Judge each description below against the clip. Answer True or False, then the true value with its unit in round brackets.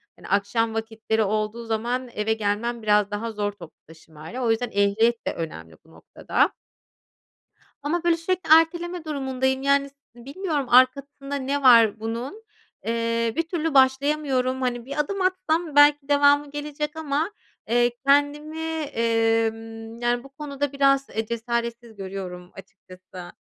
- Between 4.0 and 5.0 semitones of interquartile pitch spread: True (4.5 semitones)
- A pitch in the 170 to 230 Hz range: False (245 Hz)